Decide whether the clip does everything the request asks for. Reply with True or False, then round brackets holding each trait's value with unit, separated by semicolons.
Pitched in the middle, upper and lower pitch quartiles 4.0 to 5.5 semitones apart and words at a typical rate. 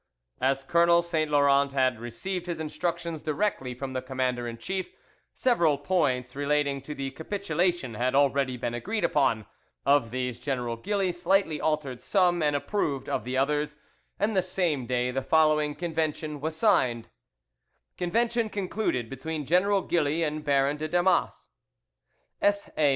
True (150 Hz; 4.8 semitones; 145 wpm)